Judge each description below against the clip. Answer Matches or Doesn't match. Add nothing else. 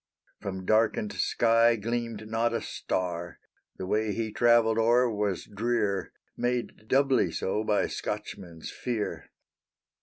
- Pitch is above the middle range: Doesn't match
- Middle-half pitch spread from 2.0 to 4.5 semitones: Matches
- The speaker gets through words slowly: Matches